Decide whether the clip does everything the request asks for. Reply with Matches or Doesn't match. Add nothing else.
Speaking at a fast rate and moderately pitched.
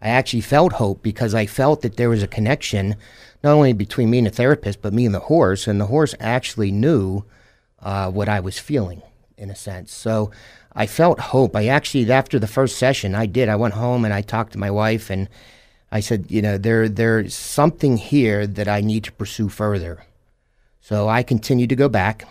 Doesn't match